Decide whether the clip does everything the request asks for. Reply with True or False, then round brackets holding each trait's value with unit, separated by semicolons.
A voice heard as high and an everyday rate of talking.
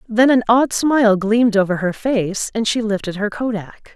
True (220 Hz; 195 wpm)